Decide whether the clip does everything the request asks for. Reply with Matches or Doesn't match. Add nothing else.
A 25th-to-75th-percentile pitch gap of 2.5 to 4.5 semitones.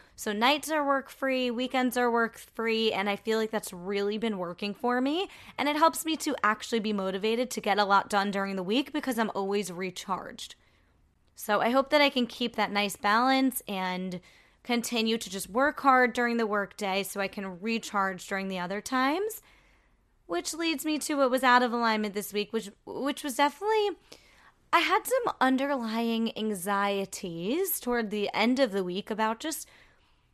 Doesn't match